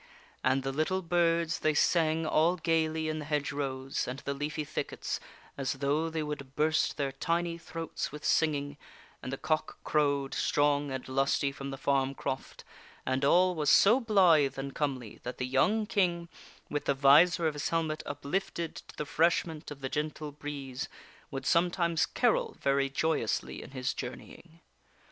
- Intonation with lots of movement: No, average, 3.1 semitones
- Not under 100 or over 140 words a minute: No, average, 170 wpm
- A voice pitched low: No, medium, 150 Hz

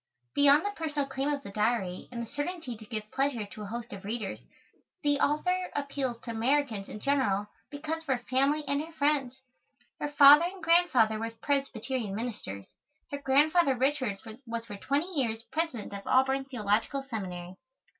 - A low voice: No, very high, 265 Hz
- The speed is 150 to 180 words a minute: Yes, average, 170 wpm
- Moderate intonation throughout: Yes, average, 4.7 semitones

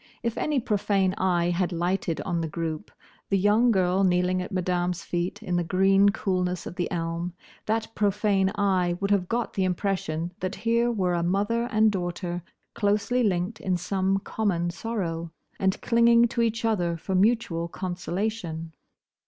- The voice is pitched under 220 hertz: Yes, high, 190 Hz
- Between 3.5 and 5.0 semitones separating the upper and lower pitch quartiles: No, average, 3.0 semitones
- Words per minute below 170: Yes, average, 160 wpm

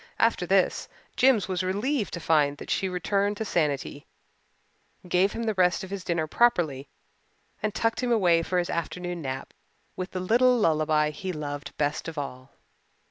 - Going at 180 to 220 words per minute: No, average, 170 wpm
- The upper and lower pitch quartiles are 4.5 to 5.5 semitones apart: Yes, average, 4.9 semitones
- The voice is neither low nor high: Yes, medium, 180 Hz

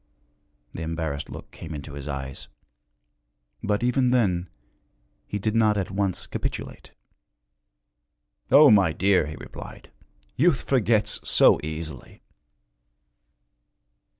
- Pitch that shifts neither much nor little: No, wide, 6.3 semitones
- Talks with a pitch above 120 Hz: No, very low, 95 Hz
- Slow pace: Yes, slow, 105 wpm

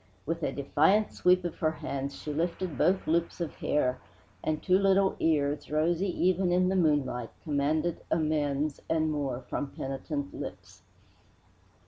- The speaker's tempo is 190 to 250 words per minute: No, average, 145 wpm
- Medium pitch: Yes, medium, 155 Hz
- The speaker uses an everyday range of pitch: Yes, average, 3.6 semitones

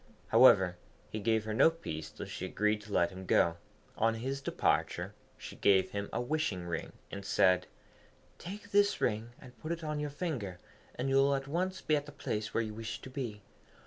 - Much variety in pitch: Yes, wide, 6.4 semitones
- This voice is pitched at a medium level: No, low, 115 Hz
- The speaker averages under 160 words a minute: No, fast, 205 wpm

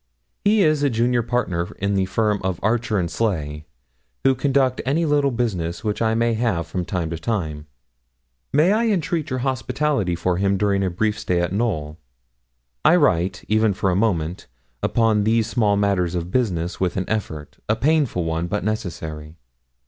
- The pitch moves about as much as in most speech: No, wide, 5.7 semitones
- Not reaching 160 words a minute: No, average, 175 wpm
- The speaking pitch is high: No, low, 105 Hz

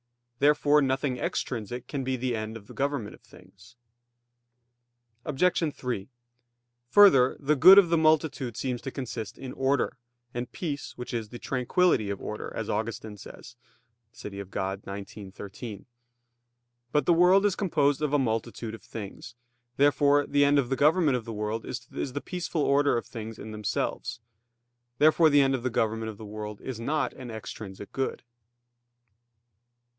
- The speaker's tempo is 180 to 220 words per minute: No, average, 160 wpm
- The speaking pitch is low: Yes, low, 125 Hz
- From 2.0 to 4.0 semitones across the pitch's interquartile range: No, average, 4.8 semitones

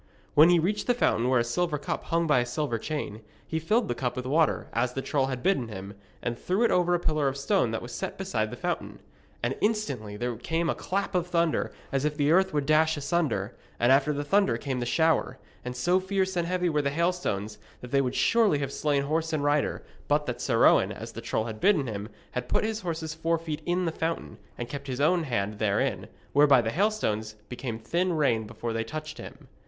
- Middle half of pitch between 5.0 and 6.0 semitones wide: Yes, wide, 5.6 semitones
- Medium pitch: Yes, medium, 145 Hz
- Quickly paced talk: Yes, fast, 230 wpm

